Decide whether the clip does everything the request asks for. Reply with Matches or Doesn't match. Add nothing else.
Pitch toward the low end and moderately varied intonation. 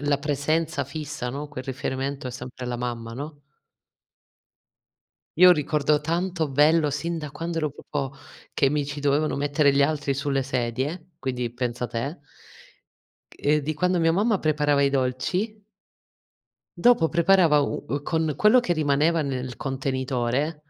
Doesn't match